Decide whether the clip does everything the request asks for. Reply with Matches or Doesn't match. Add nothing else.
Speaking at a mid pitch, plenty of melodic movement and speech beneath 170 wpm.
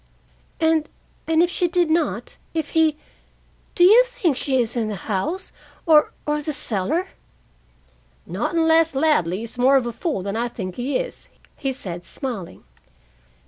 Doesn't match